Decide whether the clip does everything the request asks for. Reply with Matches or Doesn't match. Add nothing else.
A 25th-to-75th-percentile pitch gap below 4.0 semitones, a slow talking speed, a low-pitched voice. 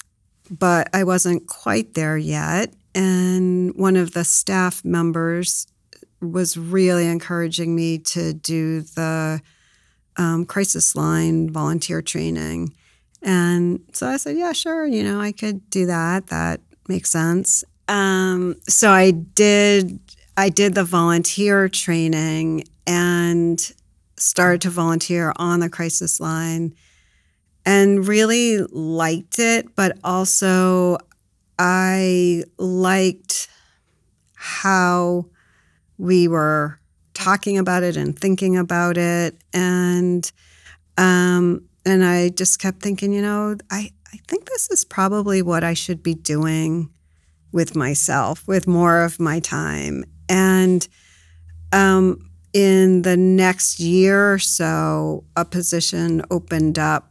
Doesn't match